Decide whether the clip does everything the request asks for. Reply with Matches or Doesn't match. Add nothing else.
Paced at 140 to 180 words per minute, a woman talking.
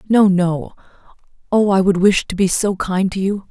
Doesn't match